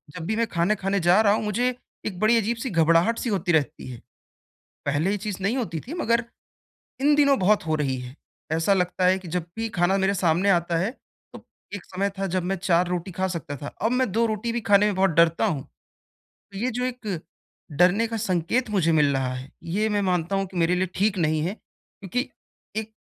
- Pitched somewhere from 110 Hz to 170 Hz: No, high, 190 Hz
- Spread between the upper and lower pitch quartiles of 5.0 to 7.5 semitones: No, average, 4.3 semitones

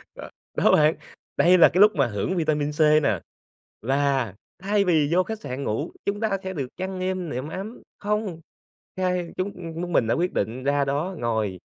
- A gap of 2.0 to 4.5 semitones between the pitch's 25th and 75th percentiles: No, average, 5.2 semitones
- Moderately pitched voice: Yes, medium, 165 Hz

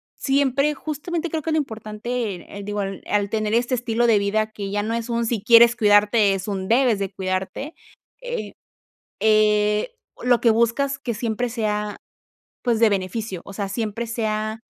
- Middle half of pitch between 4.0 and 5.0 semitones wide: No, average, 2.8 semitones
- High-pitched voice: Yes, high, 220 Hz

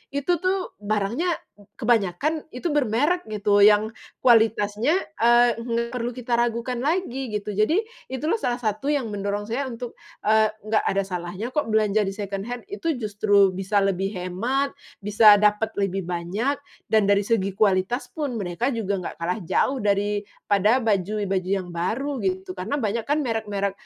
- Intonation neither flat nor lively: Yes, average, 3.7 semitones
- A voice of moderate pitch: No, high, 215 Hz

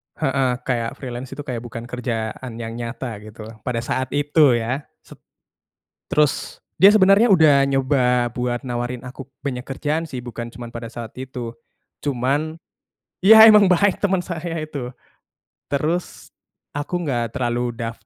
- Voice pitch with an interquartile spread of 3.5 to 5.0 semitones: Yes, average, 3.8 semitones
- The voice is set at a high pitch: No, low, 130 Hz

